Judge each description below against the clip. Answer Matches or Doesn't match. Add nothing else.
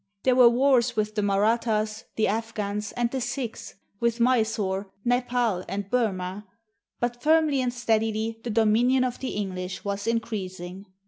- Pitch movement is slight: Doesn't match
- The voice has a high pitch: Matches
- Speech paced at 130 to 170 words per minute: Matches